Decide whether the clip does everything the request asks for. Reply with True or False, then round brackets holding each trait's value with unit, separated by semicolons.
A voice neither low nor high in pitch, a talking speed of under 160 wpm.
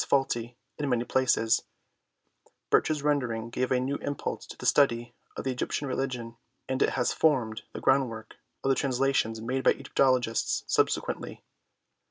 False (130 Hz; 150 wpm)